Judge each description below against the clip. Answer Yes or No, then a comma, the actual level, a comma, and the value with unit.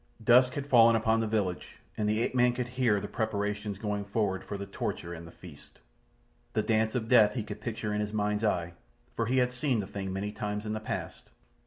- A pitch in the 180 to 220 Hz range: No, low, 105 Hz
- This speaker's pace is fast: Yes, fast, 220 wpm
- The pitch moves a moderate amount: No, narrow, 2.2 semitones